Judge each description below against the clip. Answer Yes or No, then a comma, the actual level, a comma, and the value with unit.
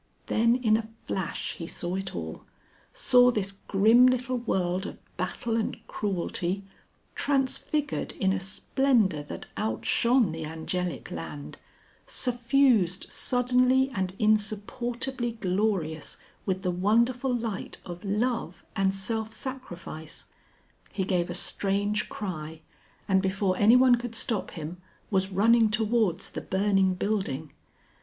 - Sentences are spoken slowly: Yes, slow, 120 wpm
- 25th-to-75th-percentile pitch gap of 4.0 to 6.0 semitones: Yes, average, 4.5 semitones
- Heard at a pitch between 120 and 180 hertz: No, high, 205 Hz